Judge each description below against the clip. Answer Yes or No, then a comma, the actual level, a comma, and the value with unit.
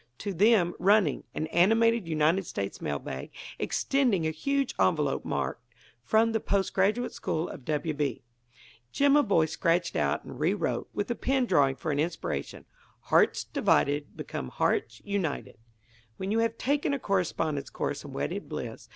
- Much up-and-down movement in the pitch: Yes, wide, 6.7 semitones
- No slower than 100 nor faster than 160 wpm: Yes, average, 155 wpm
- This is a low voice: No, medium, 185 Hz